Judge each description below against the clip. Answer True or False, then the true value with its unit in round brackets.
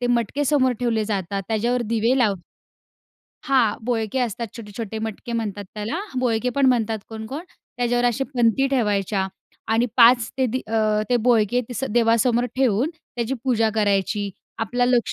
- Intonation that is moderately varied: False (2.3 semitones)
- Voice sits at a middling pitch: False (230 Hz)